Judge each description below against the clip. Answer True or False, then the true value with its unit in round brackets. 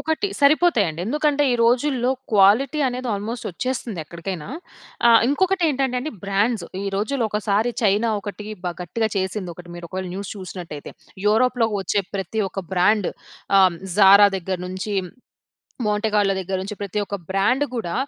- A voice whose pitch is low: False (210 Hz)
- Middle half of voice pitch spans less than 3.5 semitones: False (4.5 semitones)